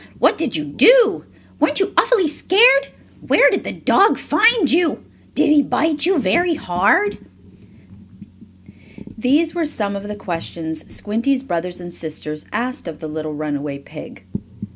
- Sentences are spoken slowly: No, average, 145 wpm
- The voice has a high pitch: Yes, very high, 255 Hz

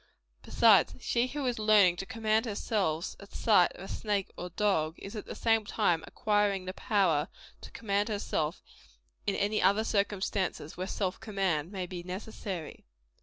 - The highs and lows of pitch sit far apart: No, average, 2.9 semitones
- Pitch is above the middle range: Yes, high, 200 Hz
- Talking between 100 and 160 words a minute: No, average, 170 wpm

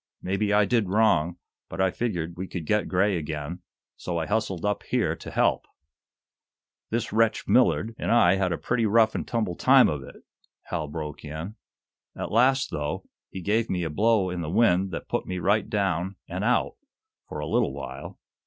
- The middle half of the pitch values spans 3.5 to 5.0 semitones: Yes, average, 4.2 semitones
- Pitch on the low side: Yes, very low, 95 Hz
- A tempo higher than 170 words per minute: Yes, average, 190 wpm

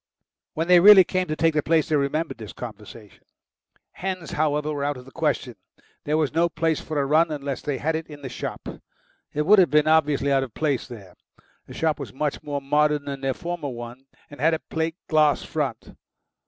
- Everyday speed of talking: No, fast, 210 wpm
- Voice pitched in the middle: Yes, medium, 150 Hz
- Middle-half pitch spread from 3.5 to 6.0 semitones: No, average, 2.7 semitones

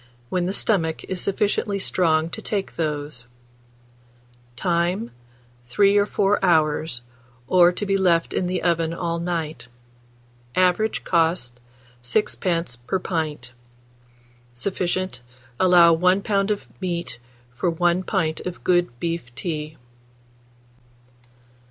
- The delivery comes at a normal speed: No, slow, 115 wpm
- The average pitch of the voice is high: No, medium, 175 Hz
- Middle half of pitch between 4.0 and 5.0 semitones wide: No, average, 2.7 semitones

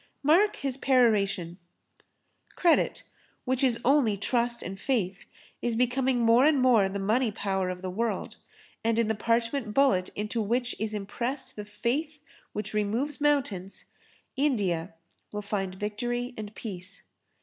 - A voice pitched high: Yes, high, 230 Hz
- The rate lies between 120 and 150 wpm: Yes, average, 140 wpm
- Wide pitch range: No, average, 4.2 semitones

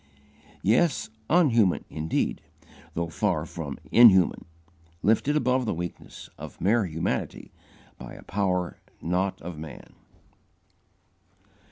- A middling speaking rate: No, slow, 100 wpm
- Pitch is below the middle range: Yes, very low, 95 Hz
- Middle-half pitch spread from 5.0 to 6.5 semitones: Yes, wide, 5.6 semitones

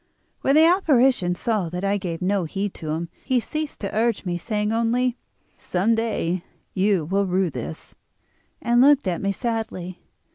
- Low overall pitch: No, high, 205 Hz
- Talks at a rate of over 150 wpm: Yes, average, 170 wpm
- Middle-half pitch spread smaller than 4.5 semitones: No, average, 4.9 semitones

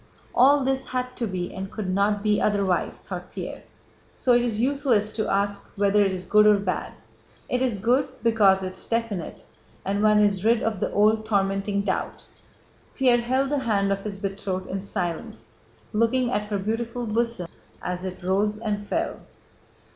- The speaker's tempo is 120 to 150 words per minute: No, average, 175 wpm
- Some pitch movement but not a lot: Yes, average, 3.1 semitones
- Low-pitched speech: No, high, 210 Hz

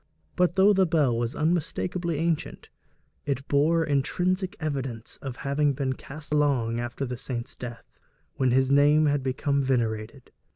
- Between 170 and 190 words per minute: No, average, 150 wpm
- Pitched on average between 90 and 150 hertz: Yes, medium, 140 Hz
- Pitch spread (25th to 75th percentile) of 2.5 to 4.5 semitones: Yes, average, 3.5 semitones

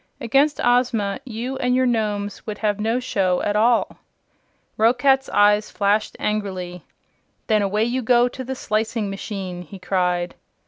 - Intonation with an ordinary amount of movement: Yes, average, 3.5 semitones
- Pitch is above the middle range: Yes, high, 215 Hz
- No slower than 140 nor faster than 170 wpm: Yes, average, 145 wpm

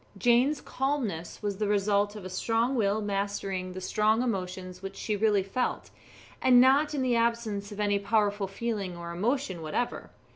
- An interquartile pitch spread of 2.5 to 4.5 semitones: Yes, average, 3.3 semitones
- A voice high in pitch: Yes, high, 205 Hz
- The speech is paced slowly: No, average, 170 wpm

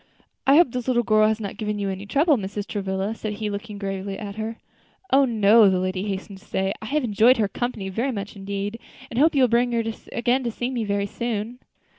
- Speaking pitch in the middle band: No, high, 215 Hz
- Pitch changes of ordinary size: Yes, average, 3.2 semitones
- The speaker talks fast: Yes, fast, 230 wpm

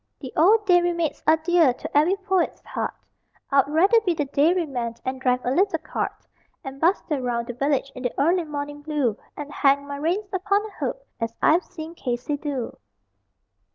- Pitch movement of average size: Yes, average, 4.6 semitones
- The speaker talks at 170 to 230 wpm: Yes, average, 190 wpm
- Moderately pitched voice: No, very high, 300 Hz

